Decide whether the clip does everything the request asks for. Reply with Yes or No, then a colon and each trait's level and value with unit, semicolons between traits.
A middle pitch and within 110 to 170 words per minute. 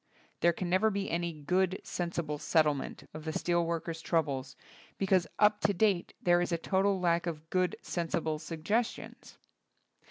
Yes: medium, 170 Hz; average, 160 wpm